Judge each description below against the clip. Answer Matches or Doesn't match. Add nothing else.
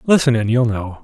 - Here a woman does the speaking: Doesn't match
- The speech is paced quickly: Matches